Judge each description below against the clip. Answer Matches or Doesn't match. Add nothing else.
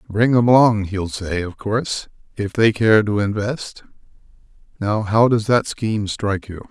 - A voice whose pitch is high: Doesn't match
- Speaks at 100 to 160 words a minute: Doesn't match